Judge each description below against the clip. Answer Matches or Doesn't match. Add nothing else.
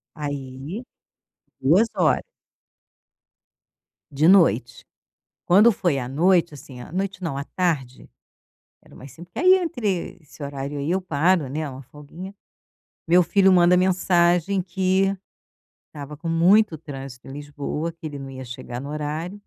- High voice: Doesn't match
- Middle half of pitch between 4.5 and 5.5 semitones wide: Matches